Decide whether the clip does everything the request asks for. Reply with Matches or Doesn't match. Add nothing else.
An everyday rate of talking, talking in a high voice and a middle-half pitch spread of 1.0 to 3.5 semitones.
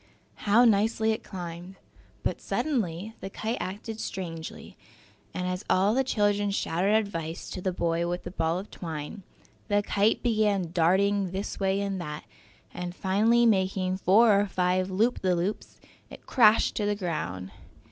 Matches